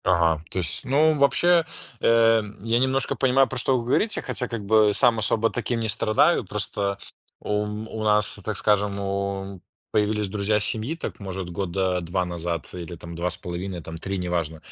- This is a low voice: Yes, low, 105 Hz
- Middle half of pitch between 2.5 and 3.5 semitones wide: No, average, 4.2 semitones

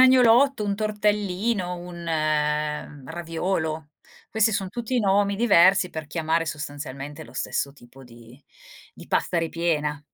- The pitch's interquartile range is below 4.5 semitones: No, average, 5.1 semitones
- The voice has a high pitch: No, medium, 175 Hz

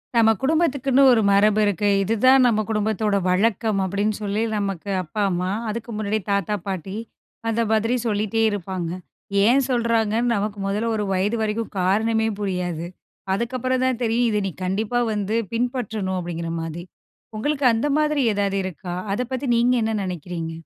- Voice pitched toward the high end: Yes, high, 215 Hz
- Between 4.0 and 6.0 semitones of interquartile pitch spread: No, average, 3.2 semitones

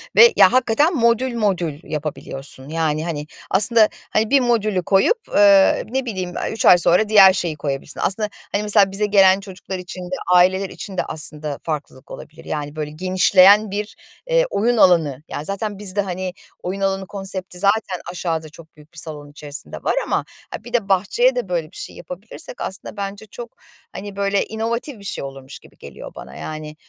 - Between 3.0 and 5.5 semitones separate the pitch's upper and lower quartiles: Yes, average, 4.8 semitones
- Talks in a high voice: Yes, high, 195 Hz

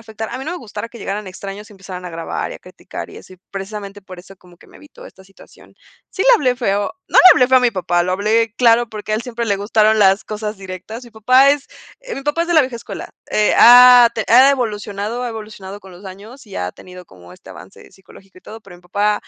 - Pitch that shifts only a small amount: No, average, 3.9 semitones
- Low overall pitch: No, high, 210 Hz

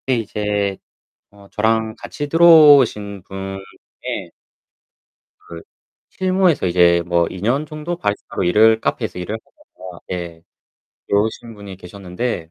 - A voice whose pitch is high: No, low, 105 Hz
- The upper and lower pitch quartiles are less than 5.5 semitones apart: Yes, average, 5.1 semitones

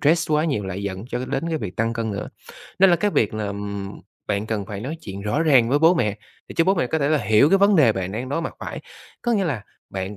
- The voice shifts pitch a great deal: Yes, wide, 7.8 semitones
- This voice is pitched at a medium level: No, low, 120 Hz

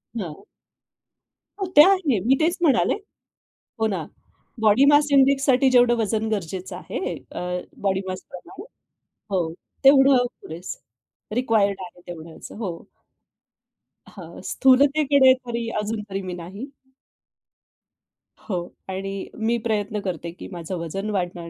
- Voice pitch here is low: No, high, 215 Hz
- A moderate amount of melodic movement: No, wide, 6.1 semitones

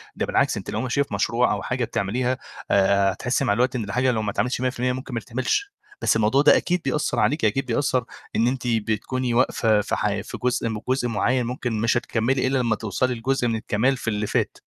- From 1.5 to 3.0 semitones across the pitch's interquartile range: Yes, narrow, 2.6 semitones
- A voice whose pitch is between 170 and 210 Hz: No, low, 120 Hz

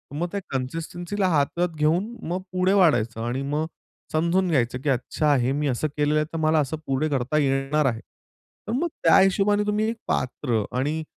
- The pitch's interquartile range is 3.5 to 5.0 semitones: Yes, average, 4.6 semitones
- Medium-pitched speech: Yes, medium, 155 Hz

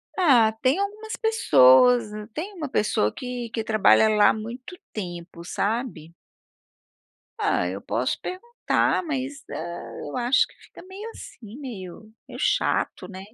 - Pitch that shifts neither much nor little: No, wide, 7.9 semitones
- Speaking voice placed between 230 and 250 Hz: Yes, high, 235 Hz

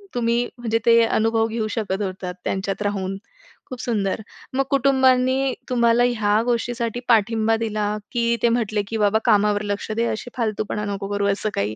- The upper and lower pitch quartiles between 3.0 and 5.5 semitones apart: No, narrow, 2.5 semitones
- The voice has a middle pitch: No, high, 225 Hz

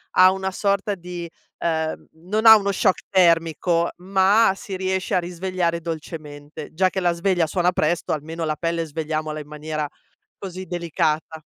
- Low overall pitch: No, medium, 170 Hz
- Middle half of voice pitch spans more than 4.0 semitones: No, average, 2.9 semitones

